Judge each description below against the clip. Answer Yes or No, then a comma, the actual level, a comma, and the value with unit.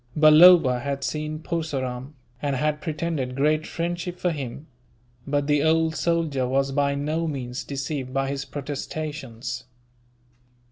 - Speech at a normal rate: No, slow, 130 wpm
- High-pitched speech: No, medium, 145 Hz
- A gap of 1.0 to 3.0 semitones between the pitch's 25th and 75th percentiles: Yes, narrow, 2.6 semitones